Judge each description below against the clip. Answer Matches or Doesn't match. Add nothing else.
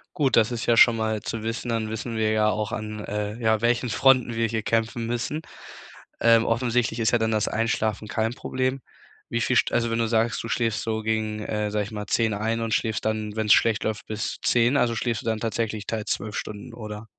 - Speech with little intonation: Matches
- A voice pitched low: Matches